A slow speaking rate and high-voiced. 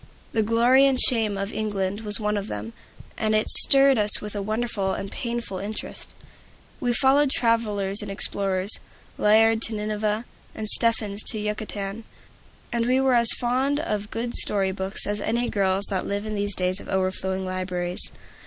No: average, 170 wpm; high, 210 Hz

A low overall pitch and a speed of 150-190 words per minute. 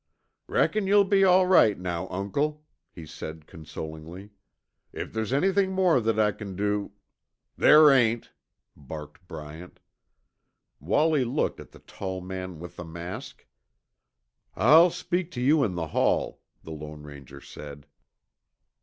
No: low, 100 Hz; slow, 135 wpm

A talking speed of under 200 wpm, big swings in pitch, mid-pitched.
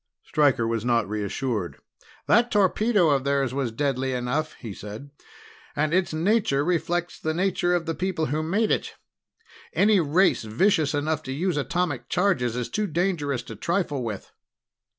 Yes: average, 155 wpm; wide, 6.0 semitones; medium, 150 Hz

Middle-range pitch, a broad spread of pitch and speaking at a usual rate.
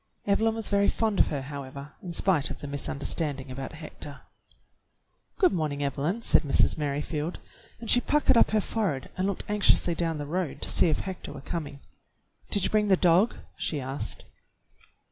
Yes: medium, 165 Hz; wide, 5.9 semitones; average, 185 wpm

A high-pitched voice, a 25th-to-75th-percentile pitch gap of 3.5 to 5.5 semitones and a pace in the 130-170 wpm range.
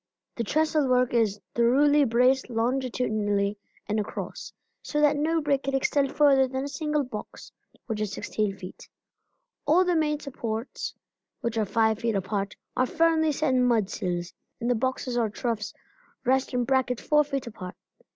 Yes: very high, 250 Hz; average, 4.6 semitones; average, 160 wpm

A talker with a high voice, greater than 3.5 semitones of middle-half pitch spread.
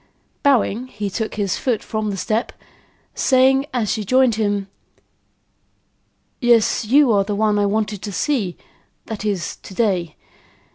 No: high, 215 Hz; average, 3.1 semitones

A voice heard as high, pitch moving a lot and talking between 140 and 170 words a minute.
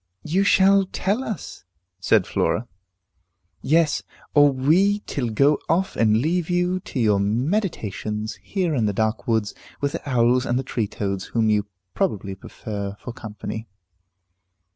No: low, 125 Hz; wide, 7.9 semitones; average, 145 wpm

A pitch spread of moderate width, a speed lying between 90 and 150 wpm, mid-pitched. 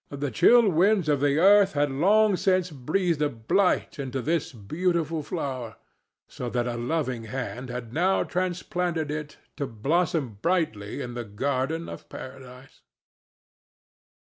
No: wide, 5.7 semitones; average, 140 wpm; medium, 145 Hz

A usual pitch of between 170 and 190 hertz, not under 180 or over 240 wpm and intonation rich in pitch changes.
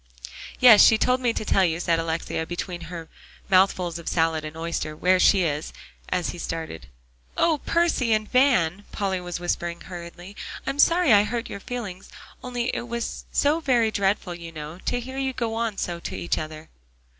Yes: medium, 185 Hz; average, 185 wpm; wide, 5.9 semitones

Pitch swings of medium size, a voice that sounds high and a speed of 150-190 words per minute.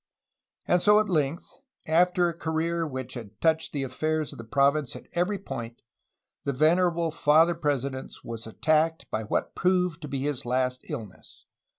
No: average, 4.4 semitones; medium, 155 Hz; average, 165 wpm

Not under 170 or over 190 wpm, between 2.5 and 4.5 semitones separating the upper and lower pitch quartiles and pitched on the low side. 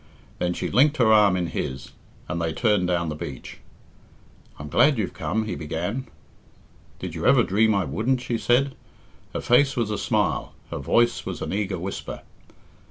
No: average, 175 wpm; average, 5.3 semitones; low, 105 Hz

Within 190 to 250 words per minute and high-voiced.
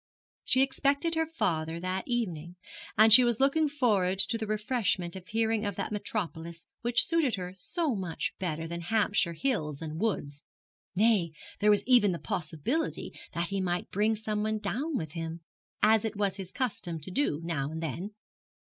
No: average, 175 wpm; high, 205 Hz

